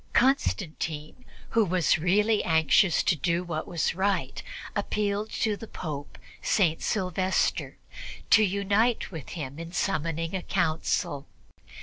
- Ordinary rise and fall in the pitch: Yes, average, 4.1 semitones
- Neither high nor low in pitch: Yes, medium, 180 Hz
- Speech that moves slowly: Yes, slow, 120 wpm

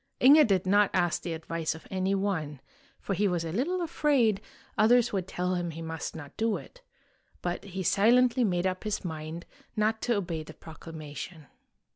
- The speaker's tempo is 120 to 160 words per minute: No, average, 180 wpm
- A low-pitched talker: No, medium, 185 Hz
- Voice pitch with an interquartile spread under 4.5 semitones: No, average, 4.9 semitones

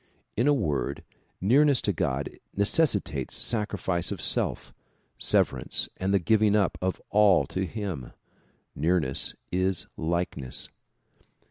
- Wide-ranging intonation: No, average, 4.2 semitones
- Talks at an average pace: No, slow, 120 wpm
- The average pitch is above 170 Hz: No, very low, 95 Hz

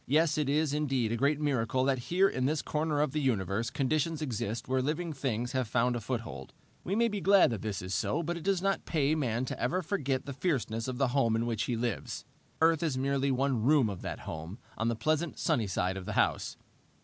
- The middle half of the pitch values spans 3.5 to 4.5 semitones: No, average, 4.9 semitones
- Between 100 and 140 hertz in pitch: Yes, low, 135 Hz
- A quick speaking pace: Yes, fast, 230 wpm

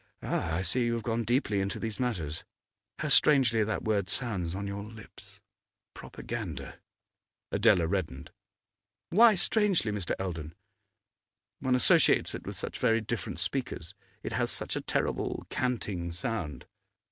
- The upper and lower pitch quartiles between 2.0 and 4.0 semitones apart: No, average, 5.1 semitones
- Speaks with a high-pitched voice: No, low, 105 Hz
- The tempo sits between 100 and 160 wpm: Yes, average, 140 wpm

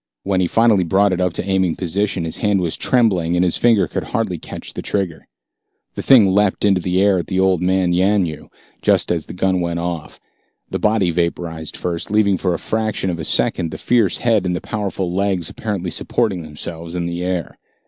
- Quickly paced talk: Yes, fast, 210 wpm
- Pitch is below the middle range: Yes, very low, 95 Hz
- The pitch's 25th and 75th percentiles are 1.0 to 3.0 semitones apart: Yes, average, 2.7 semitones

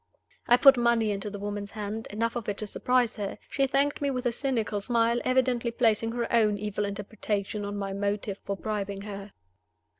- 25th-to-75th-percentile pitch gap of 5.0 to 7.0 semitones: No, average, 2.8 semitones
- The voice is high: Yes, high, 215 Hz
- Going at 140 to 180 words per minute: No, average, 190 wpm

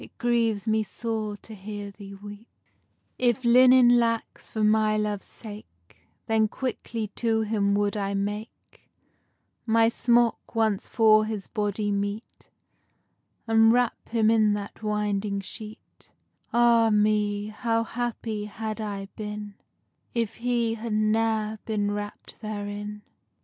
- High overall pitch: Yes, high, 215 Hz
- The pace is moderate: No, slow, 110 wpm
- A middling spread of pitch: No, narrow, 1.6 semitones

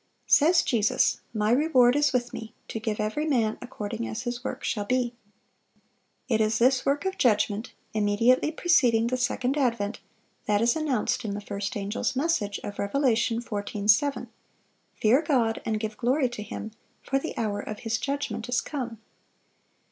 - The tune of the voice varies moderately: Yes, average, 3.4 semitones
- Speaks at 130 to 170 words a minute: Yes, average, 165 wpm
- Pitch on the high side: Yes, high, 235 Hz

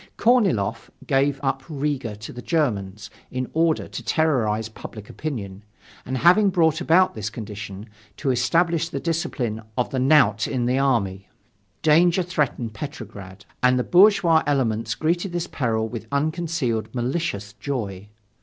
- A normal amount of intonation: No, wide, 6.6 semitones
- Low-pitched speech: Yes, low, 130 Hz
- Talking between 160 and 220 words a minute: No, average, 140 wpm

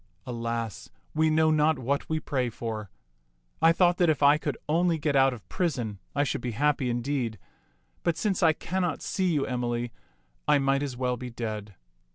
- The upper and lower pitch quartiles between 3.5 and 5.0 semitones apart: Yes, average, 4.7 semitones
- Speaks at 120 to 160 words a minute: No, average, 185 wpm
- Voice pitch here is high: No, medium, 140 Hz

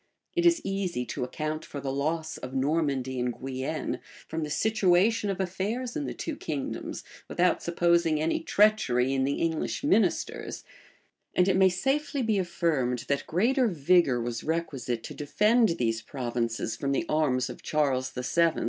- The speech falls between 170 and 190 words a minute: No, average, 160 wpm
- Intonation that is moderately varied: No, wide, 6.4 semitones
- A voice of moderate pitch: Yes, medium, 160 Hz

